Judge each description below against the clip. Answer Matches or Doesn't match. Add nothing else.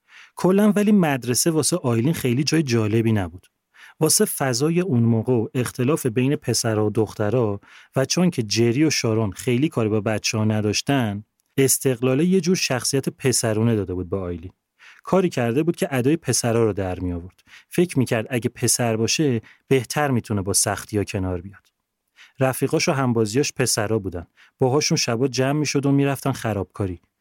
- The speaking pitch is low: Matches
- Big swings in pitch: Doesn't match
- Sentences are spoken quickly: Matches